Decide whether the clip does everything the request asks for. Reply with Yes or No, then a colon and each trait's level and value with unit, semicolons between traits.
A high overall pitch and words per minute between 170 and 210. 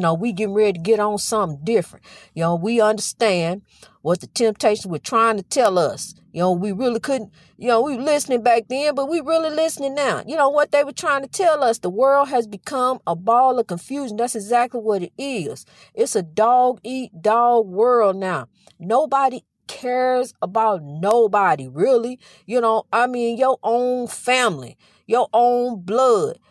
Yes: high, 235 Hz; average, 185 wpm